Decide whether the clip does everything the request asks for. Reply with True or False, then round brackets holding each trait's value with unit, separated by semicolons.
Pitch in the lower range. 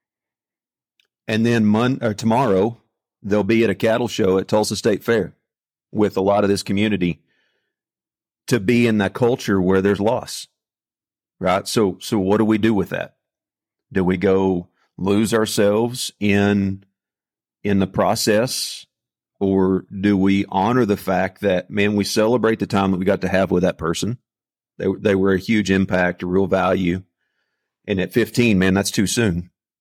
True (100 Hz)